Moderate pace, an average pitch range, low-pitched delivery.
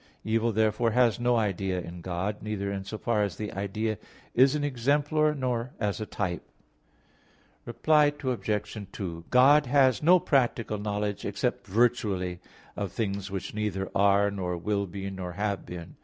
Yes: average, 155 wpm; average, 3.8 semitones; low, 105 Hz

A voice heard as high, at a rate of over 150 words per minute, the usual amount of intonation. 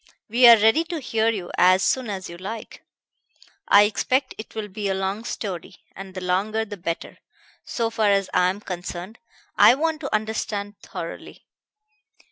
Yes: high, 210 Hz; average, 170 wpm; average, 3.0 semitones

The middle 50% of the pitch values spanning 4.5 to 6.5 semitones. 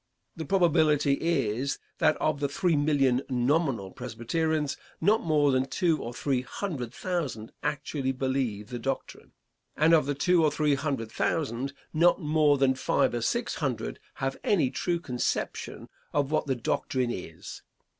No: average, 3.8 semitones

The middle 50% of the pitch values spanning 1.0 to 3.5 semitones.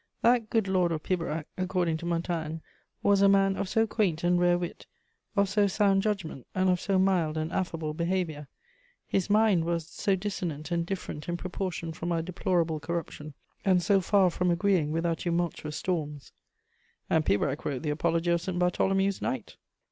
Yes: average, 3.0 semitones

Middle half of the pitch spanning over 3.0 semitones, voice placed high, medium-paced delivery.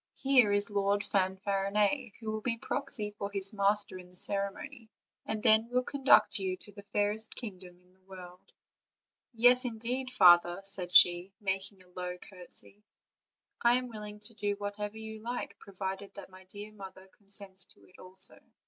No: narrow, 2.5 semitones; high, 205 Hz; average, 175 wpm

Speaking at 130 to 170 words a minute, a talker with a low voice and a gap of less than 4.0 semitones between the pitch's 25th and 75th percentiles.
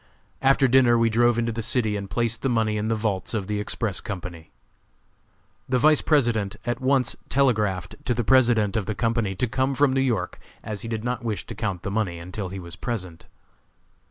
No: fast, 205 wpm; low, 115 Hz; average, 3.3 semitones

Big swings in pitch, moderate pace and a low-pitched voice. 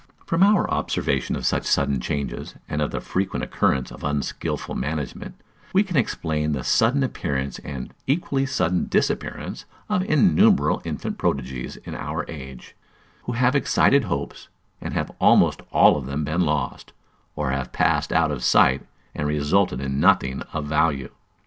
Yes: wide, 8.5 semitones; average, 155 wpm; very low, 75 Hz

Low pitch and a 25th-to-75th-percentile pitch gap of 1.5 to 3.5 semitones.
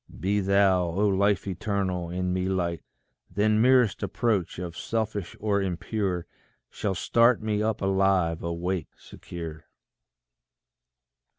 Yes: very low, 95 Hz; average, 2.8 semitones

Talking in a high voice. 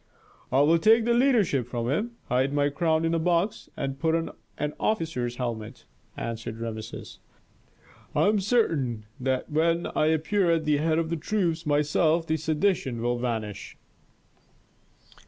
No: medium, 155 Hz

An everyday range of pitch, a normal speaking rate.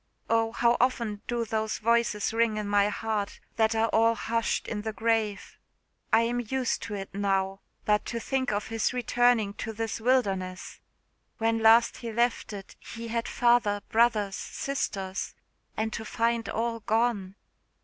No: narrow, 2.1 semitones; average, 160 wpm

